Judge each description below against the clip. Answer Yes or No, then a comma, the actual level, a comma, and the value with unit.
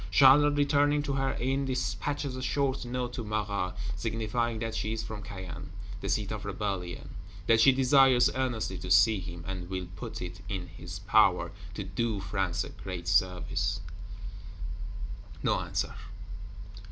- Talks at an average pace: Yes, average, 155 wpm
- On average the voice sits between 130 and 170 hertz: No, low, 105 Hz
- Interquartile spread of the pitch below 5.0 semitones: No, average, 5.3 semitones